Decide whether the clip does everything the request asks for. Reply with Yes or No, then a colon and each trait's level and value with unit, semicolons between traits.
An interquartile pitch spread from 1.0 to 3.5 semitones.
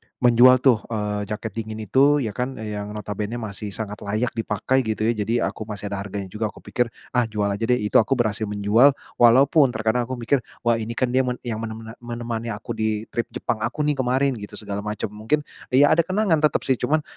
Yes: average, 3.1 semitones